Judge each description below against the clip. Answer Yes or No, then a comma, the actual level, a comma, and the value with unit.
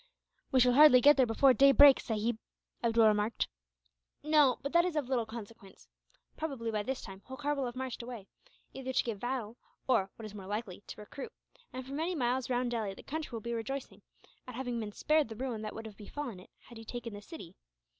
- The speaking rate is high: Yes, fast, 215 wpm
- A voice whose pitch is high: Yes, high, 245 Hz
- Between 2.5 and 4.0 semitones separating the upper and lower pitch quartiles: Yes, average, 3.5 semitones